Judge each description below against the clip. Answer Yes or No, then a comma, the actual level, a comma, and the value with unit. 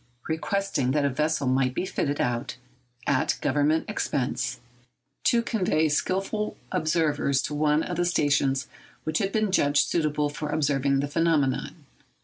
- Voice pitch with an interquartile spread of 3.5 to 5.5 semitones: No, average, 3.1 semitones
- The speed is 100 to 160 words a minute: Yes, average, 140 wpm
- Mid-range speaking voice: Yes, medium, 150 Hz